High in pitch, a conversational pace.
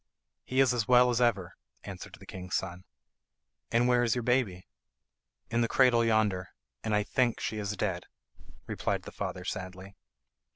No: low, 110 Hz; average, 165 wpm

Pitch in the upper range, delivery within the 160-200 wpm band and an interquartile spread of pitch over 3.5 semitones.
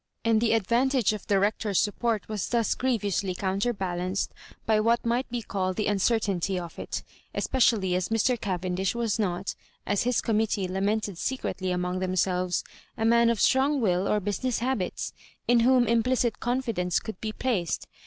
Yes: high, 215 Hz; average, 170 wpm; average, 3.9 semitones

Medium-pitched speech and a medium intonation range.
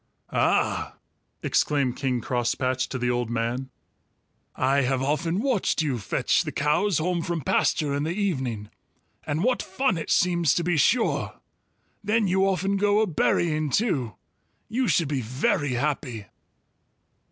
No: medium, 150 Hz; wide, 6.6 semitones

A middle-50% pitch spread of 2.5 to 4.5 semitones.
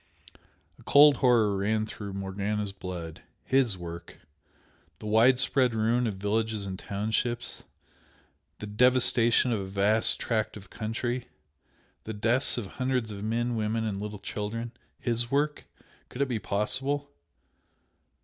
Yes: average, 3.1 semitones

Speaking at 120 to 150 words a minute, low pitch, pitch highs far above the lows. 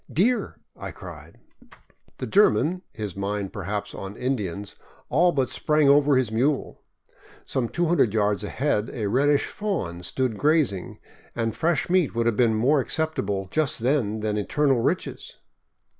Yes: average, 145 wpm; low, 125 Hz; wide, 6.2 semitones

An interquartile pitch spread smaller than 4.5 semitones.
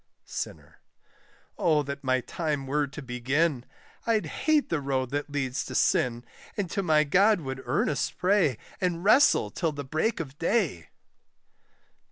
No: average, 5.1 semitones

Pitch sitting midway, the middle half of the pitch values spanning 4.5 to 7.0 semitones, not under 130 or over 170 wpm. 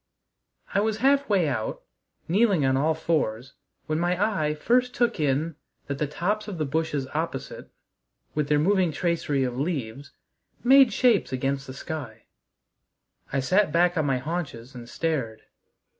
Yes: medium, 155 Hz; wide, 5.5 semitones; average, 150 wpm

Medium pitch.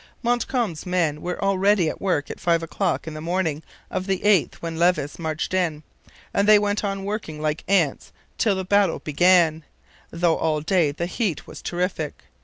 Yes: medium, 175 Hz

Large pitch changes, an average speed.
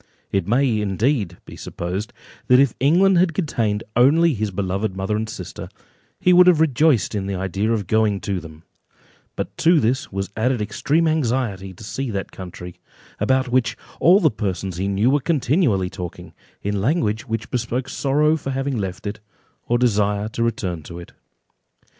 Yes: wide, 5.7 semitones; average, 170 wpm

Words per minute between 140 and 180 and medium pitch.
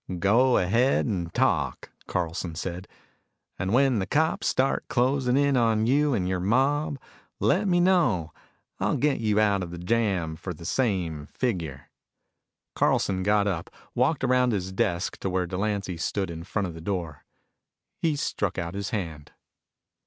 No: average, 160 wpm; low, 100 Hz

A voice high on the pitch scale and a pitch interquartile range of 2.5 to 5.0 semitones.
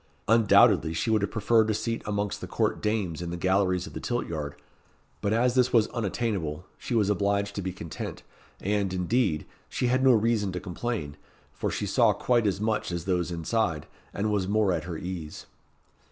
No: low, 100 Hz; average, 4.0 semitones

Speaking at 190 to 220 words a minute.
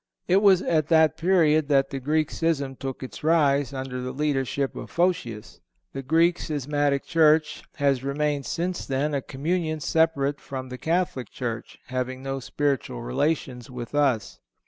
No: average, 155 wpm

